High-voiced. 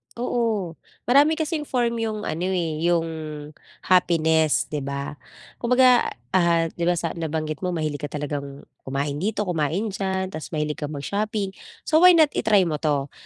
No: medium, 175 Hz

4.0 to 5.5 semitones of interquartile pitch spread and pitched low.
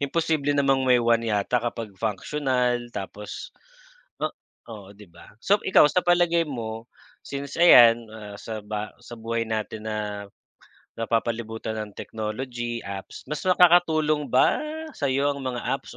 Yes: average, 4.5 semitones; low, 120 Hz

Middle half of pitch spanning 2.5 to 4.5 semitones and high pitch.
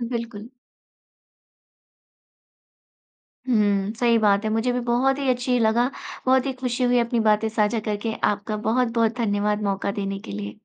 Yes: average, 2.8 semitones; high, 225 Hz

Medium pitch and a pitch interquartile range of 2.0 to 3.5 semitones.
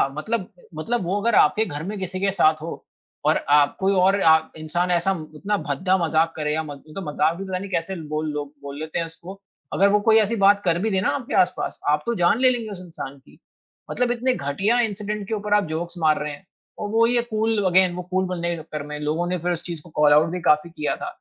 No: medium, 180 Hz; average, 4.7 semitones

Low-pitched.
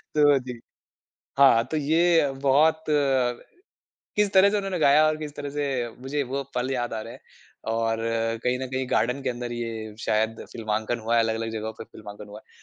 Yes: low, 130 Hz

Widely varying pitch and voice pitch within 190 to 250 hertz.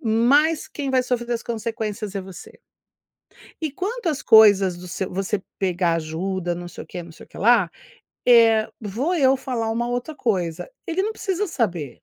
Yes: wide, 5.9 semitones; high, 225 Hz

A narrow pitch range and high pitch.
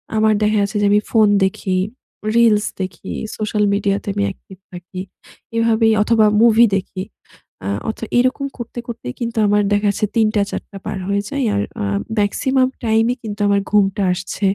Yes: narrow, 2.2 semitones; high, 210 Hz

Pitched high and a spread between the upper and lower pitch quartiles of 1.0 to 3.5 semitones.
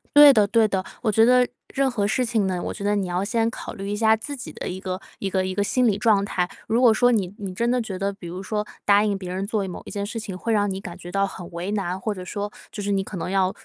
Yes: high, 200 Hz; average, 2.8 semitones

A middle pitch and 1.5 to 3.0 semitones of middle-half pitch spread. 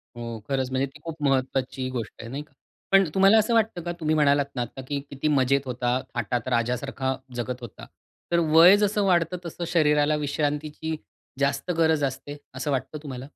No: medium, 145 Hz; average, 3.7 semitones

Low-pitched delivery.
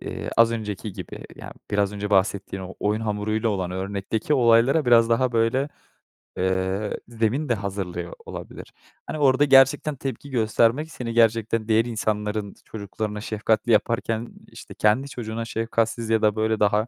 Yes: low, 110 Hz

